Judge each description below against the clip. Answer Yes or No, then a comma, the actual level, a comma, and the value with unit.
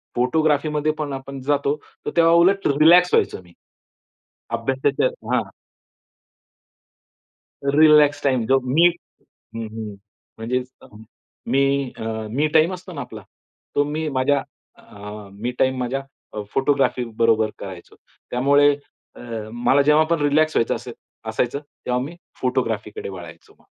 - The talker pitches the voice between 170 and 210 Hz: No, low, 135 Hz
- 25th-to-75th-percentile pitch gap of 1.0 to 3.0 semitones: No, average, 3.9 semitones